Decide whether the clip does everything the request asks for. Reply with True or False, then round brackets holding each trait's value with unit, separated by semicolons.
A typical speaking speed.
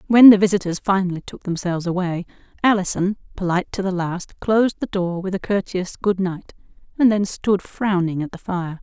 True (185 wpm)